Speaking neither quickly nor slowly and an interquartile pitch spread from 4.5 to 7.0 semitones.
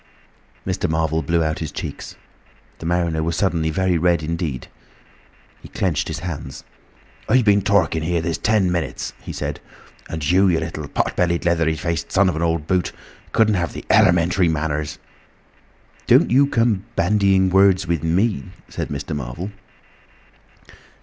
No: average, 155 wpm; average, 2.9 semitones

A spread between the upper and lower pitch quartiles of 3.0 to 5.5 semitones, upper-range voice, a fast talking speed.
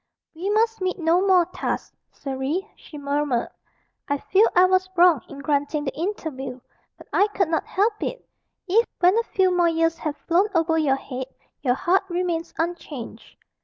No: average, 4.4 semitones; very high, 335 Hz; average, 170 wpm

